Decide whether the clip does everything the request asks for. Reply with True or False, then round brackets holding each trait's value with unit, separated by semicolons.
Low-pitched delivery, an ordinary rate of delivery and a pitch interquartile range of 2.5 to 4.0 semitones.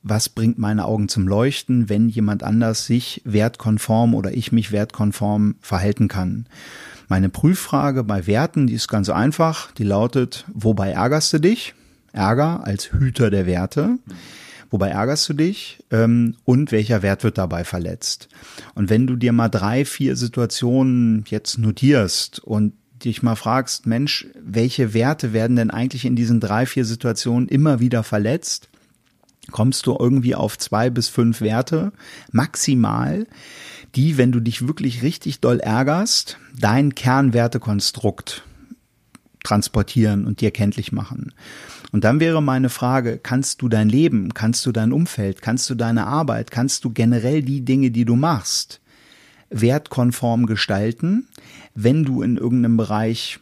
True (120 Hz; 145 wpm; 3.4 semitones)